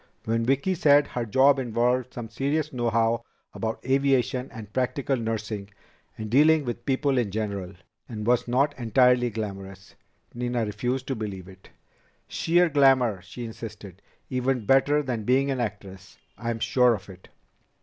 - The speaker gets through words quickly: No, average, 150 wpm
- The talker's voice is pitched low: Yes, low, 120 Hz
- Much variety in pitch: No, average, 3.7 semitones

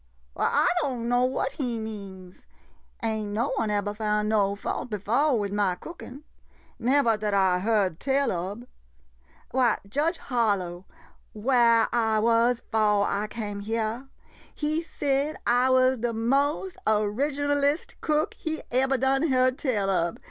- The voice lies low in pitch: No, high, 230 Hz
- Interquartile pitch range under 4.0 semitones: No, average, 4.3 semitones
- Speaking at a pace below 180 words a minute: Yes, average, 155 wpm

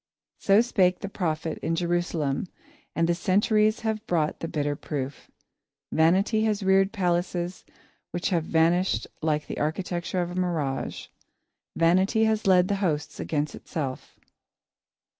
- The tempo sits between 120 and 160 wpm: Yes, slow, 135 wpm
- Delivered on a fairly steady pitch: No, average, 3.3 semitones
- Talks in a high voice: No, medium, 175 Hz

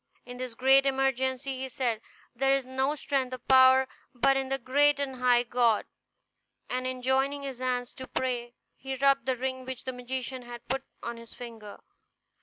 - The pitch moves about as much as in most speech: No, narrow, 1.4 semitones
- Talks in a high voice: Yes, very high, 260 Hz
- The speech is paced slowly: No, average, 185 wpm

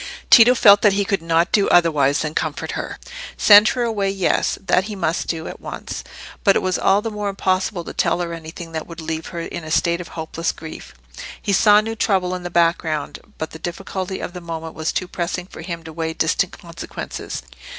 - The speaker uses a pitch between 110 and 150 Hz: No, medium, 175 Hz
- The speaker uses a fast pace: Yes, fast, 210 wpm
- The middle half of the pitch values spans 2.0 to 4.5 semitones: Yes, average, 3.3 semitones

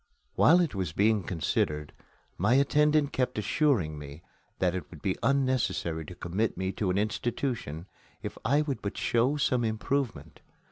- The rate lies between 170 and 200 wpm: No, average, 155 wpm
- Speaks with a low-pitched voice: Yes, low, 110 Hz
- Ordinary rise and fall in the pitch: No, wide, 7.3 semitones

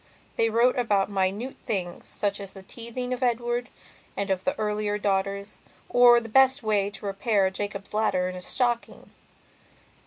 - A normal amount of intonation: Yes, average, 3.4 semitones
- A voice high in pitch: Yes, high, 210 Hz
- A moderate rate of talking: Yes, average, 165 wpm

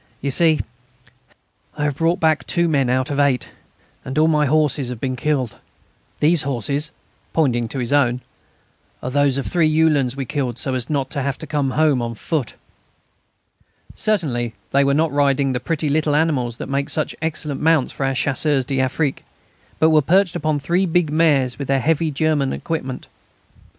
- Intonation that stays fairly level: No, average, 3.1 semitones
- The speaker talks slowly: No, average, 180 wpm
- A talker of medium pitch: Yes, medium, 145 Hz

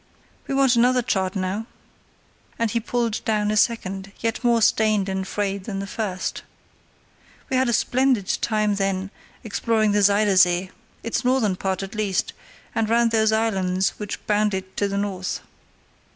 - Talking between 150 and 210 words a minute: Yes, average, 165 wpm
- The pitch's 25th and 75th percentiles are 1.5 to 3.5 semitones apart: Yes, average, 2.9 semitones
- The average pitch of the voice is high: Yes, high, 210 Hz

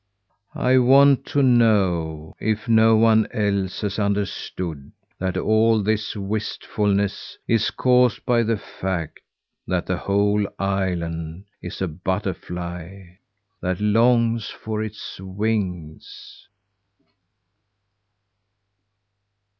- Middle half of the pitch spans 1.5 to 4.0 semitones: Yes, average, 3.2 semitones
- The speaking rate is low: Yes, slow, 95 wpm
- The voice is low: Yes, low, 100 Hz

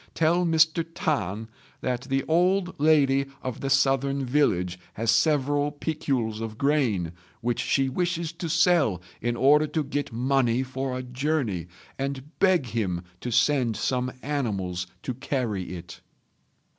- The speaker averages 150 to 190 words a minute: No, average, 140 wpm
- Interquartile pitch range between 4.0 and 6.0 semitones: Yes, average, 4.5 semitones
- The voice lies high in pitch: No, low, 135 Hz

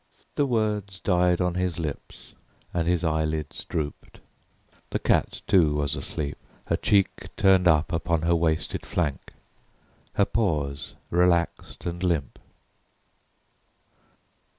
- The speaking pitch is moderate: No, very low, 85 Hz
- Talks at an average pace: No, slow, 115 wpm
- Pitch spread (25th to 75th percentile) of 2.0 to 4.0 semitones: Yes, average, 2.8 semitones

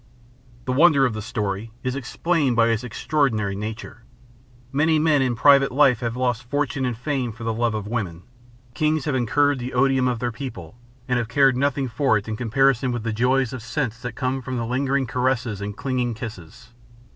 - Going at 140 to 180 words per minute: No, average, 195 wpm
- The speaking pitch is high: No, low, 125 Hz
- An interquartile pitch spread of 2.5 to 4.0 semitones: Yes, average, 3.1 semitones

